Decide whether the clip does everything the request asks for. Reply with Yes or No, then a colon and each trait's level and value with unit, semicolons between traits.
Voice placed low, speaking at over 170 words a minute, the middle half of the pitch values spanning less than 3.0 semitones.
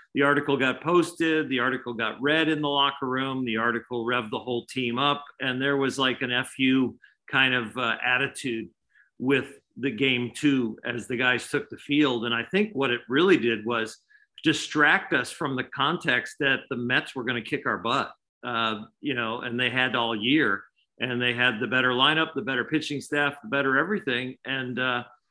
Yes: low, 130 Hz; average, 200 wpm; narrow, 2.6 semitones